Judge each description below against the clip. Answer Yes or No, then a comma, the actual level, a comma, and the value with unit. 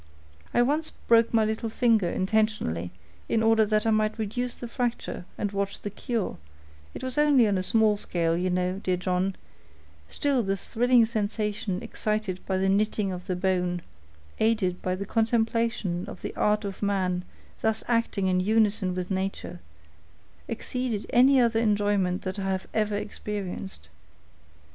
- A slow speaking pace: No, average, 160 wpm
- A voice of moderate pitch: No, high, 210 Hz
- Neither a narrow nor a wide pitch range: Yes, average, 3.2 semitones